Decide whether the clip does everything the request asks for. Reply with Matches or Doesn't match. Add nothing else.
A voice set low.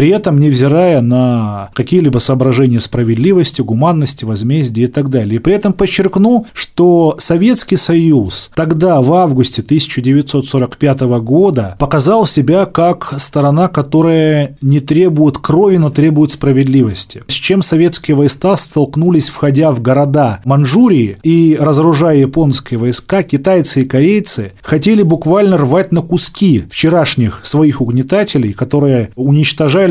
Doesn't match